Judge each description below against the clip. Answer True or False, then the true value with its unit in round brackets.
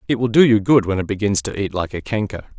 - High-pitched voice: False (105 Hz)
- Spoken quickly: True (300 wpm)